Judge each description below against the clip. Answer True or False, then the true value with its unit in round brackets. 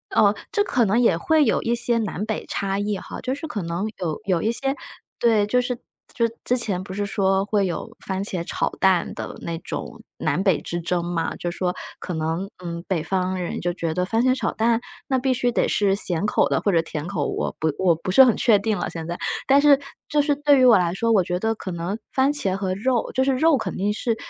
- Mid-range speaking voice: False (200 Hz)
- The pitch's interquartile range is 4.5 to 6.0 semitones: True (5.1 semitones)